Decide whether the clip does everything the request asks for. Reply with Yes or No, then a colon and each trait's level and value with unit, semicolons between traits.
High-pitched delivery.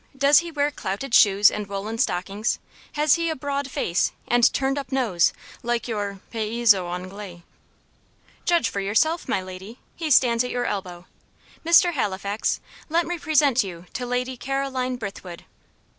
Yes: high, 240 Hz